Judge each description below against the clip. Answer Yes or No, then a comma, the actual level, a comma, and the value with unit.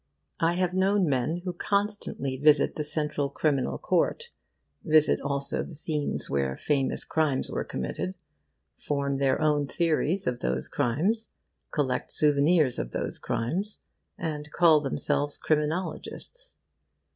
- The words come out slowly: Yes, slow, 125 wpm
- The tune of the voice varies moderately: Yes, average, 3.9 semitones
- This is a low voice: No, medium, 150 Hz